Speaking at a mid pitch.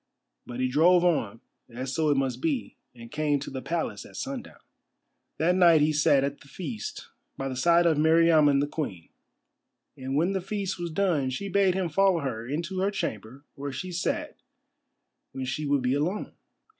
Yes: medium, 150 Hz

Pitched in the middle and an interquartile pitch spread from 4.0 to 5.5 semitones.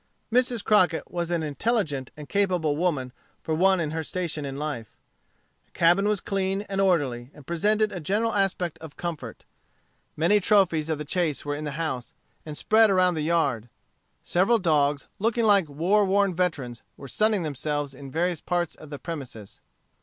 Yes: medium, 170 Hz; average, 4.9 semitones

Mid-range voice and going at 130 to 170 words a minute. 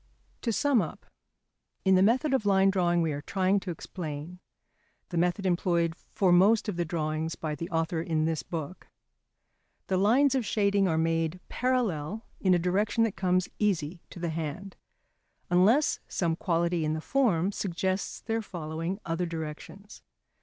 Yes: medium, 180 Hz; average, 165 wpm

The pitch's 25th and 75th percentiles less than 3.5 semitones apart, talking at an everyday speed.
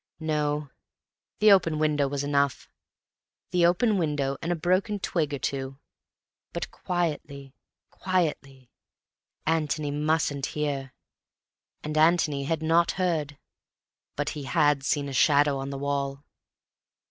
No: average, 2.7 semitones; slow, 125 wpm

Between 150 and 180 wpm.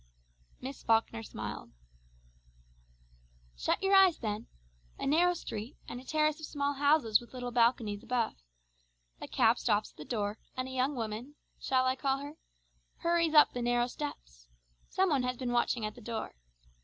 Yes: average, 170 wpm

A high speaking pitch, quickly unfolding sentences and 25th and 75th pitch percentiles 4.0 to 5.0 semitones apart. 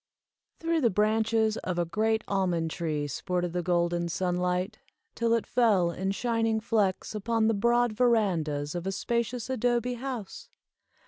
No: high, 210 Hz; average, 145 wpm; average, 4.5 semitones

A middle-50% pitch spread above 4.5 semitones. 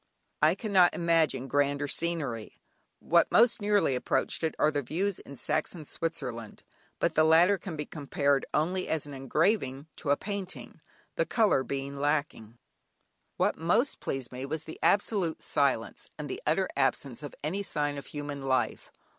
No: average, 4.0 semitones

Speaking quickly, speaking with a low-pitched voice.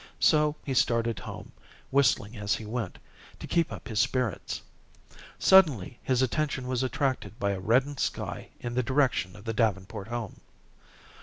No: average, 155 wpm; low, 120 Hz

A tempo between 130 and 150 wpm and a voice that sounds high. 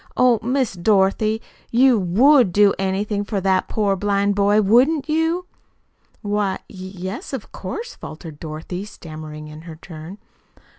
Yes: average, 140 wpm; high, 200 Hz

